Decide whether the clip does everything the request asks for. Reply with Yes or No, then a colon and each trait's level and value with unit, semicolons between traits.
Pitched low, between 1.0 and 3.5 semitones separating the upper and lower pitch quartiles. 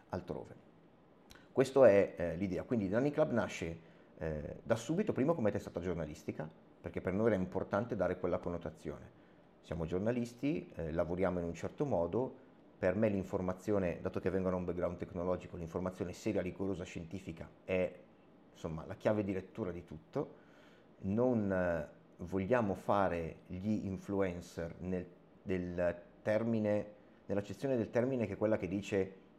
Yes: very low, 95 Hz; average, 2.8 semitones